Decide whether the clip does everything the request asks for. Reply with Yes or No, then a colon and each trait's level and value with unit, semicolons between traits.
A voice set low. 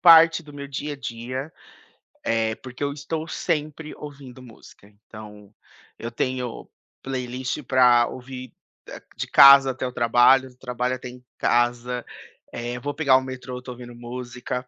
Yes: low, 125 Hz